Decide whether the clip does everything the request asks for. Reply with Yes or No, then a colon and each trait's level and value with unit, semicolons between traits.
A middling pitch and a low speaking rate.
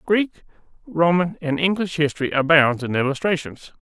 Yes: medium, 160 Hz; slow, 125 wpm